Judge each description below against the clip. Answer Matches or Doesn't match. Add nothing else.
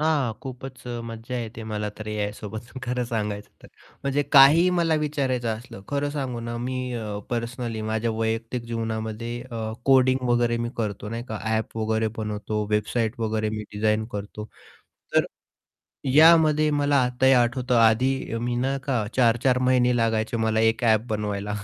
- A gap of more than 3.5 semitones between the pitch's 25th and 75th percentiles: Doesn't match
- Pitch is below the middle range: Matches